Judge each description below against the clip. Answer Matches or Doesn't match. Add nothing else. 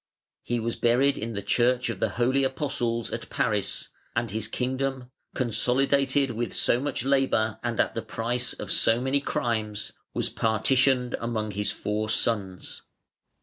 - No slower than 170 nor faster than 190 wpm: Doesn't match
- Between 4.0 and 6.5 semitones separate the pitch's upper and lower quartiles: Doesn't match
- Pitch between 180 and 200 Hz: Doesn't match